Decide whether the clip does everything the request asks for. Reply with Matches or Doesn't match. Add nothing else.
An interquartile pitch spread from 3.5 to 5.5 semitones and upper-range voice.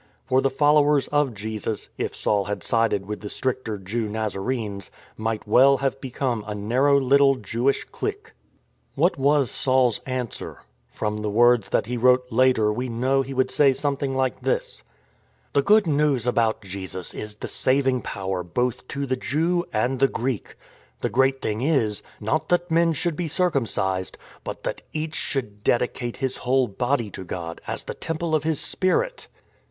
Doesn't match